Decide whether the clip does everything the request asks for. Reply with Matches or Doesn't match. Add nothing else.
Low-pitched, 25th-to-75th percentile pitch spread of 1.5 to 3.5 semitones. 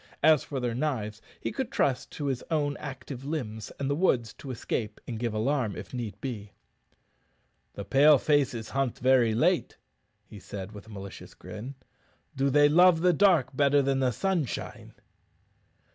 Doesn't match